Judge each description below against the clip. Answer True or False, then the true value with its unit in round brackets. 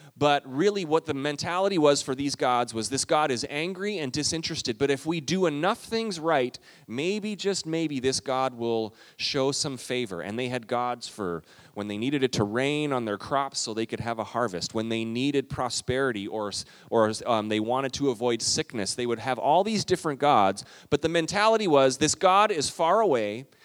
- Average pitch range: True (4.8 semitones)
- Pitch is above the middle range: False (135 Hz)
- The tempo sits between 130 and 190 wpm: False (205 wpm)